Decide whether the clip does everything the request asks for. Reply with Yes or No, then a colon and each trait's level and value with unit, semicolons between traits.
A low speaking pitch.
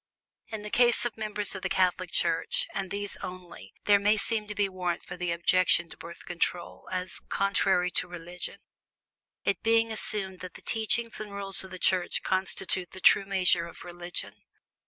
No: medium, 185 Hz